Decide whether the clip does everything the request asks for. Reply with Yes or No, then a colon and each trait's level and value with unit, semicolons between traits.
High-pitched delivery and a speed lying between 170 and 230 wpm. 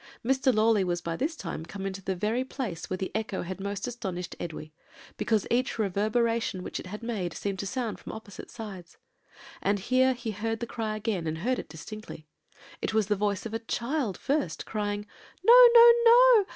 Yes: high, 215 Hz; average, 195 wpm